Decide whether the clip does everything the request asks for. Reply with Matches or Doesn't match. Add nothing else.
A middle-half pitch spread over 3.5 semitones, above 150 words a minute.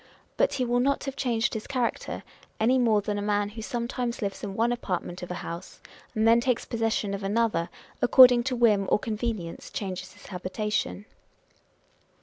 Doesn't match